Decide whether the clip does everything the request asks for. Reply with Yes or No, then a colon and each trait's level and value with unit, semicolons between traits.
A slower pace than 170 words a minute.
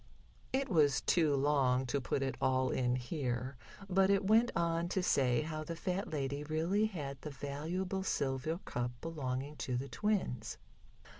Yes: average, 160 wpm